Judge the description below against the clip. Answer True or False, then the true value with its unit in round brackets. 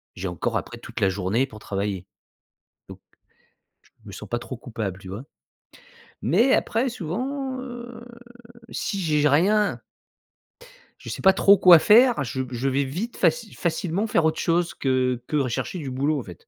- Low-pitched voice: False (150 Hz)